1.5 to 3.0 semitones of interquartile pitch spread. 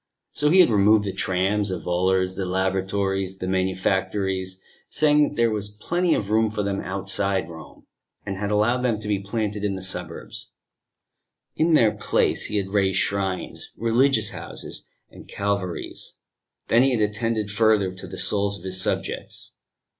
Yes: narrow, 2.4 semitones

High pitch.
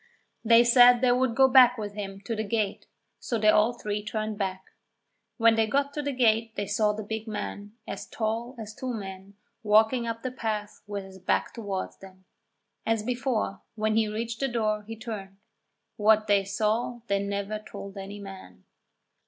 Yes: high, 215 Hz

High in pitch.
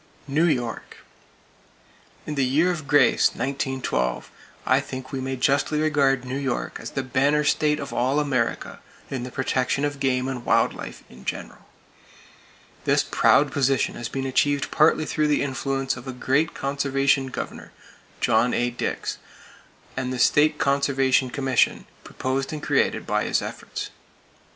No: low, 135 Hz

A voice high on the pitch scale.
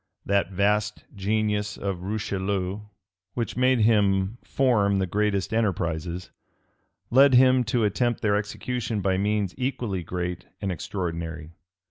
No: low, 100 Hz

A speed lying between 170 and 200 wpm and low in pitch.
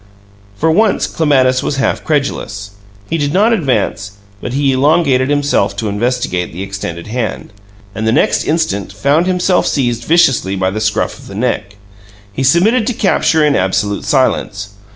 No: average, 160 wpm; low, 130 Hz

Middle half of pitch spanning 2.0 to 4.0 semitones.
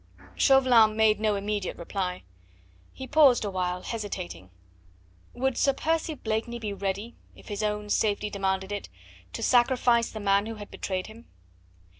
Yes: average, 3.1 semitones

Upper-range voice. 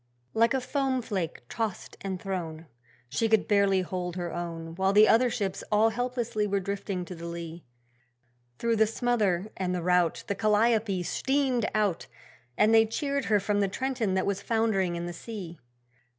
Yes: high, 200 Hz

